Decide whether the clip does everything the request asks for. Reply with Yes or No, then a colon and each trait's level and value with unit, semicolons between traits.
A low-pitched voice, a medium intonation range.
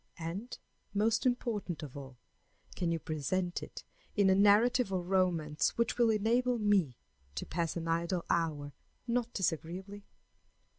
No: medium, 185 Hz; average, 4.6 semitones